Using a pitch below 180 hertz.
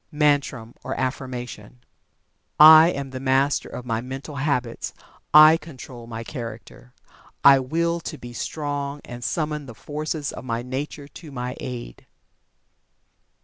Yes: low, 135 Hz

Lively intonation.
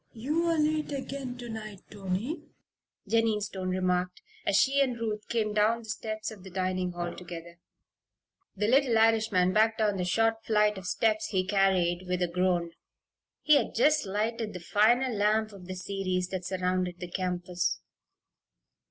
No: average, 3.6 semitones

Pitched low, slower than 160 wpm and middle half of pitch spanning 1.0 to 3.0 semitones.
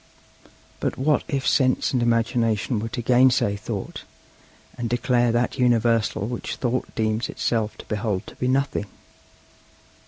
Yes: low, 120 Hz; slow, 135 wpm; narrow, 2.4 semitones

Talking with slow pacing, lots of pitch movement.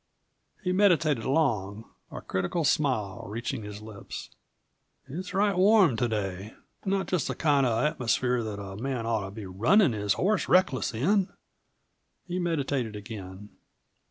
No: average, 150 wpm; wide, 8.4 semitones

